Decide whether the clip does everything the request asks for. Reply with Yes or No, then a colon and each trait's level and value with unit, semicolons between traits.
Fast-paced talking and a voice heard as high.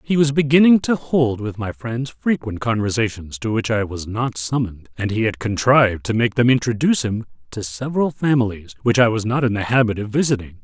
No: fast, 210 wpm; low, 120 Hz